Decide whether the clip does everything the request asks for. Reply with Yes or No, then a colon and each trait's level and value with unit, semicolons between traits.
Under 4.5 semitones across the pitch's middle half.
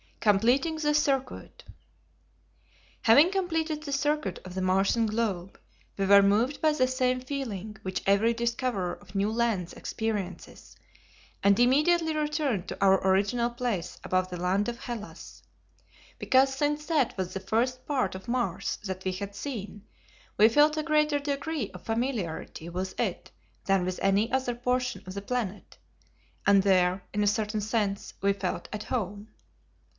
No: average, 5.3 semitones